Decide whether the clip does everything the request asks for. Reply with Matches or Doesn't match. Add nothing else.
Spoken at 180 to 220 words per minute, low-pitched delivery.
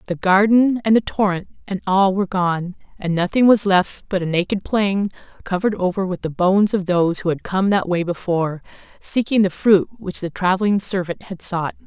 Doesn't match